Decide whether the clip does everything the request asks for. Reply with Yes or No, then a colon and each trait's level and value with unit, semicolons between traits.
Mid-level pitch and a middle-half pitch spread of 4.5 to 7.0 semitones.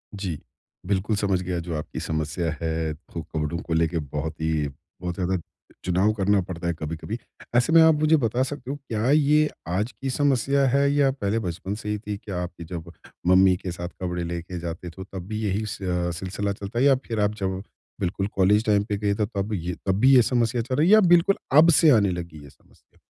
No: very low, 95 Hz; average, 5.3 semitones